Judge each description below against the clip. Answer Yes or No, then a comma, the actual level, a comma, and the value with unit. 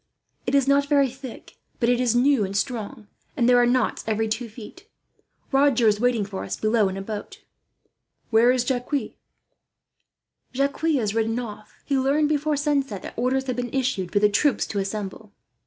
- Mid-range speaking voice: No, high, 245 Hz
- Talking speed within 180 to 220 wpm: Yes, average, 185 wpm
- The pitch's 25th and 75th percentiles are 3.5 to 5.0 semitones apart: Yes, average, 4.1 semitones